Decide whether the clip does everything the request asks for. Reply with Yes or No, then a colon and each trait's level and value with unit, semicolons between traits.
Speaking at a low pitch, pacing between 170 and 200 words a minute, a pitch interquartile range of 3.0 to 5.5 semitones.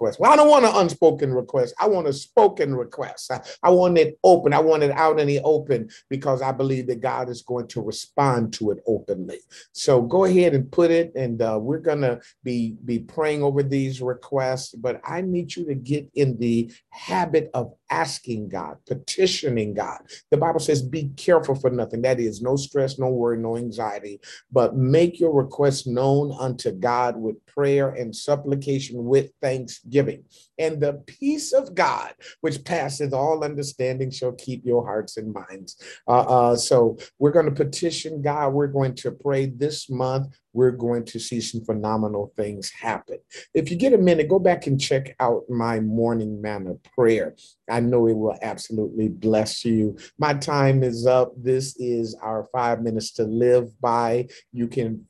Yes: low, 130 Hz; average, 185 wpm; average, 4.0 semitones